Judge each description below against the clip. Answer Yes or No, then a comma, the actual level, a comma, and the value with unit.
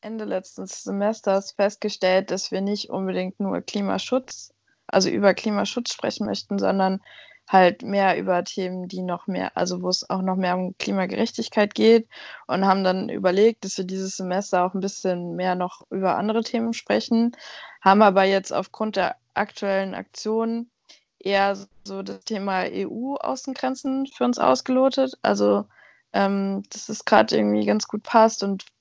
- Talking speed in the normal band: Yes, average, 155 wpm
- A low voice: No, high, 195 Hz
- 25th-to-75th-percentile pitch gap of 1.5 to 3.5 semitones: Yes, average, 3.2 semitones